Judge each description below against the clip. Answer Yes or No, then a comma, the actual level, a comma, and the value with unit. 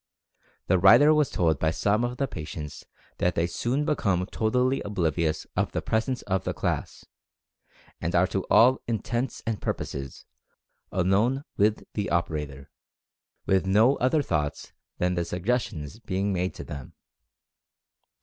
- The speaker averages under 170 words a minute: Yes, average, 145 wpm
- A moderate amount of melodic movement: No, wide, 5.9 semitones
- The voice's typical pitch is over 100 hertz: No, very low, 95 Hz